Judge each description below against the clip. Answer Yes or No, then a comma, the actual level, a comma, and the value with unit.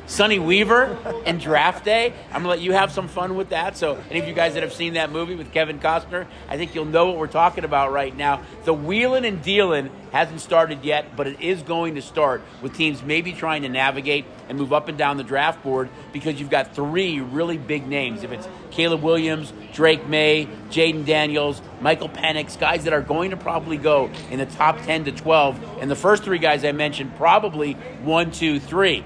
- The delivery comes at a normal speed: No, fast, 220 wpm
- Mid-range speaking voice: Yes, medium, 155 Hz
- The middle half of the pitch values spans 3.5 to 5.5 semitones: No, average, 2.8 semitones